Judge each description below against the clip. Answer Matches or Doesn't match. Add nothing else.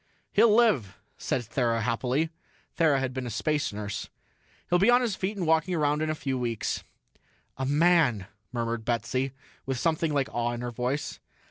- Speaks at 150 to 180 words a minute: Matches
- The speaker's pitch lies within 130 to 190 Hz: Matches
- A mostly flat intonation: Doesn't match